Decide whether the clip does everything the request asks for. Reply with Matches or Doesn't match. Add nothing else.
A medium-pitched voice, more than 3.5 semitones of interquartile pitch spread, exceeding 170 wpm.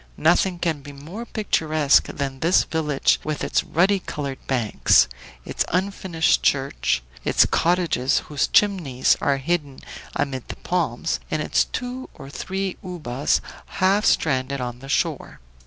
Doesn't match